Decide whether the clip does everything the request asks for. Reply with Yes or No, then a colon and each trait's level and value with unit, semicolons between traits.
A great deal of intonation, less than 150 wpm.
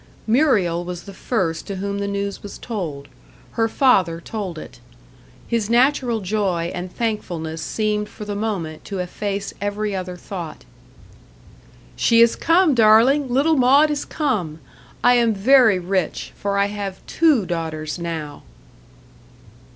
No: average, 4.7 semitones; average, 140 wpm